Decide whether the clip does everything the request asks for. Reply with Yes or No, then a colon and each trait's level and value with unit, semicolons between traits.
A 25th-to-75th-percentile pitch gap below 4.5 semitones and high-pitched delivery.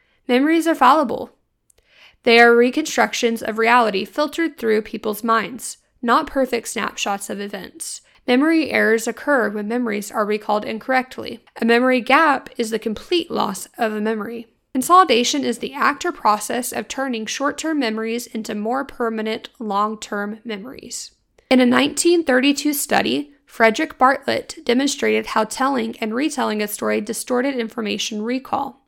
Yes: average, 3.7 semitones; high, 240 Hz